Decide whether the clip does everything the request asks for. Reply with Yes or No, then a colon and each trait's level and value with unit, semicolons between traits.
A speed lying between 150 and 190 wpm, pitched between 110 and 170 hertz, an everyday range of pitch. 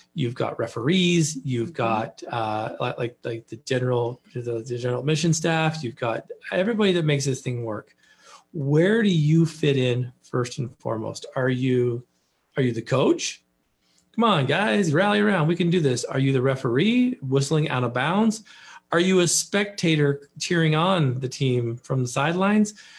No: average, 170 wpm; medium, 140 Hz; wide, 6.0 semitones